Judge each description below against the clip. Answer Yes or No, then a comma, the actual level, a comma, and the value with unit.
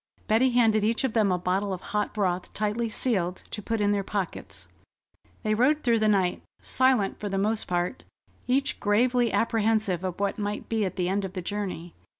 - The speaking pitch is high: Yes, high, 210 Hz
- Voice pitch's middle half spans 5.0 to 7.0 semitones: No, average, 2.9 semitones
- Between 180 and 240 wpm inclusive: Yes, average, 195 wpm